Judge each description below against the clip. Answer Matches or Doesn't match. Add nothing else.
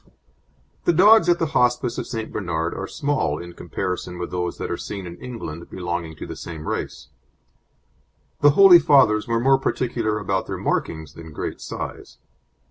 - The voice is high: Doesn't match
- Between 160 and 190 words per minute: Matches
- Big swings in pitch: Matches